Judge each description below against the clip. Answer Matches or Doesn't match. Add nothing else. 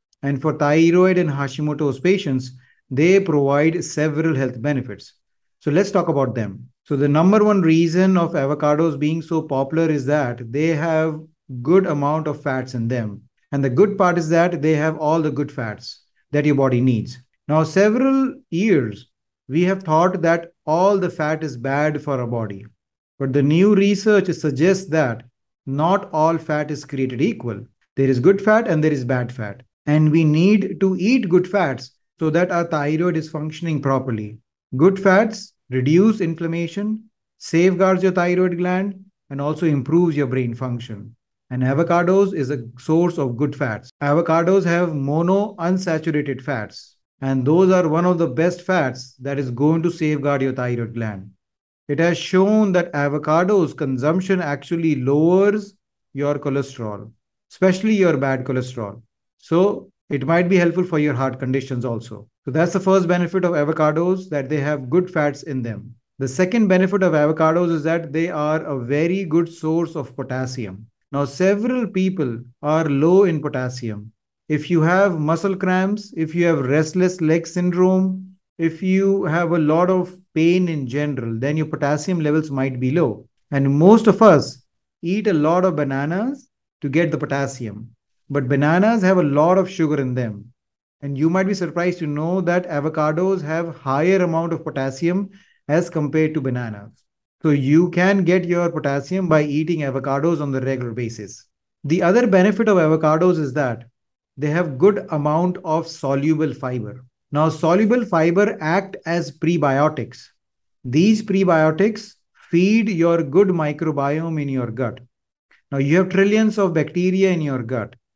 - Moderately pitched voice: Matches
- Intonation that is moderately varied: Matches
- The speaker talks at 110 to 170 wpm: Matches